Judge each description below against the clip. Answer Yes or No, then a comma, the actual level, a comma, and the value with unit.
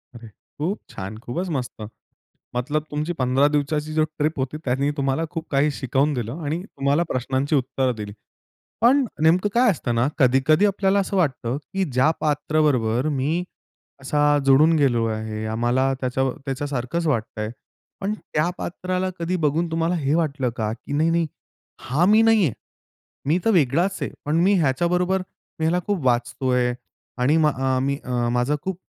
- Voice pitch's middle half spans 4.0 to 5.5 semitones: Yes, average, 4.9 semitones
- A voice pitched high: No, medium, 145 Hz